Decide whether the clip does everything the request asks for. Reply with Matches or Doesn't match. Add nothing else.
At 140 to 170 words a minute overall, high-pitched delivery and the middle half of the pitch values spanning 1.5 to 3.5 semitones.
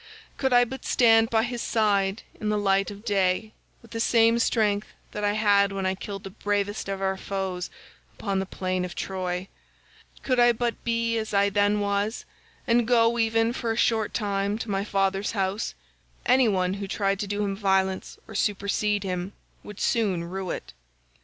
Doesn't match